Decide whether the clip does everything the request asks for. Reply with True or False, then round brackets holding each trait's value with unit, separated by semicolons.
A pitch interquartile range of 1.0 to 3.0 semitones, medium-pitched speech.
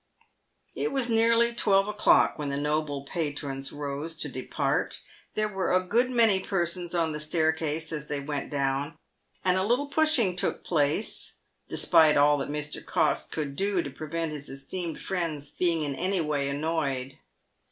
False (4.5 semitones; 160 Hz)